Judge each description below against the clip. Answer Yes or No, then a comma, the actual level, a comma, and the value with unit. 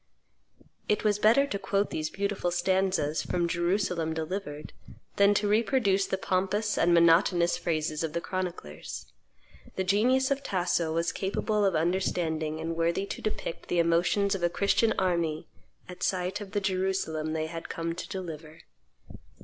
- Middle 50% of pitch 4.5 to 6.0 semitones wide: No, average, 3.2 semitones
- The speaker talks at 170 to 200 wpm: No, average, 155 wpm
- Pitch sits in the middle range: Yes, medium, 180 Hz